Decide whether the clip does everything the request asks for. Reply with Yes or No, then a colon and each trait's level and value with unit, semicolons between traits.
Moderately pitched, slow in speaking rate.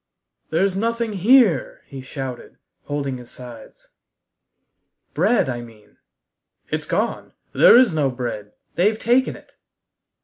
Yes: medium, 145 Hz; slow, 115 wpm